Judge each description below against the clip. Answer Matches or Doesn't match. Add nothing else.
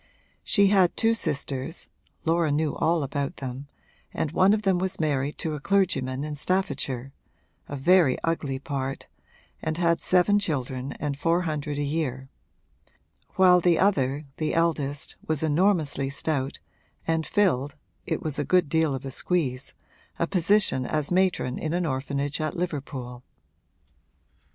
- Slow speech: Doesn't match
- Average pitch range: Matches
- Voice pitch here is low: Doesn't match